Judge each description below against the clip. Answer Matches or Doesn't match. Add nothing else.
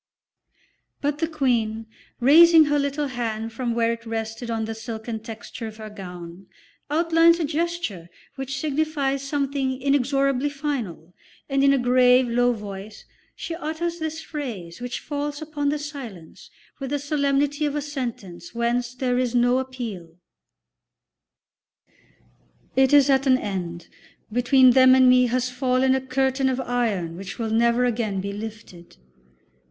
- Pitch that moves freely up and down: Doesn't match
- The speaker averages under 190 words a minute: Matches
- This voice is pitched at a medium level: Doesn't match